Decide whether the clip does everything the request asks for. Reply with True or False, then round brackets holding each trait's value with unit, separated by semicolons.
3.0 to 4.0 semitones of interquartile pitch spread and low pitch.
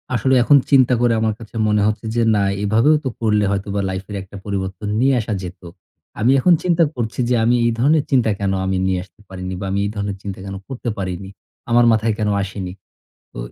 True (3.7 semitones; 105 Hz)